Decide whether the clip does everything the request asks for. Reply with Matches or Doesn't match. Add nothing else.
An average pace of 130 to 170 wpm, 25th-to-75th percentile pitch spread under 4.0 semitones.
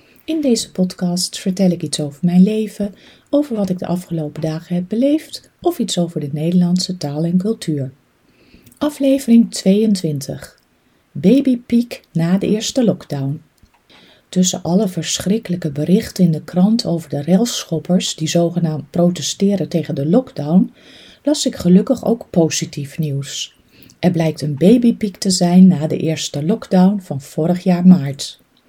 Doesn't match